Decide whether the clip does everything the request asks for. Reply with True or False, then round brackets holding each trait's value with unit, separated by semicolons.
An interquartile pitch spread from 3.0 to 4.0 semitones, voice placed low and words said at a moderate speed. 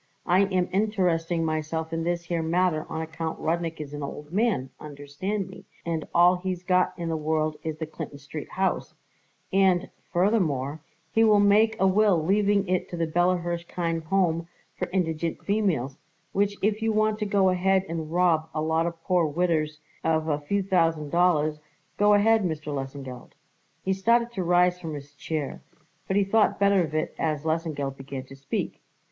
False (3.6 semitones; 170 Hz; 180 wpm)